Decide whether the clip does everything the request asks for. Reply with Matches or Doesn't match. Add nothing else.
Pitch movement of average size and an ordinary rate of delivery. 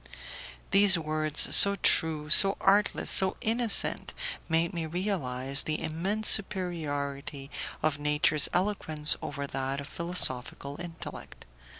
Doesn't match